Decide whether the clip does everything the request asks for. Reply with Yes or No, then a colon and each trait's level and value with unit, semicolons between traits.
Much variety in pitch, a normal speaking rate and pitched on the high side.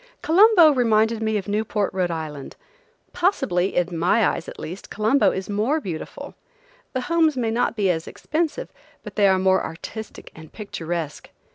Yes: wide, 5.8 semitones; average, 150 wpm; high, 210 Hz